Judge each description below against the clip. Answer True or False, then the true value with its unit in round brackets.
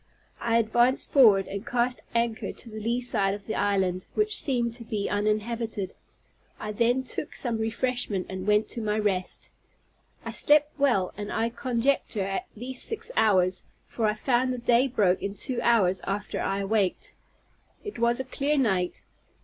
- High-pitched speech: True (225 Hz)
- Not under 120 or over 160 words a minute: False (170 wpm)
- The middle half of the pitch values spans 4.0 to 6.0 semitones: False (3.5 semitones)